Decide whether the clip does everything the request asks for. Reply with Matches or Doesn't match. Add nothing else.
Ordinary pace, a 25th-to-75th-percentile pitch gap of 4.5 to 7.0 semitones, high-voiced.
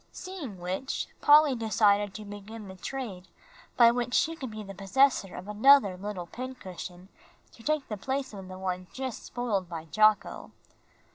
Matches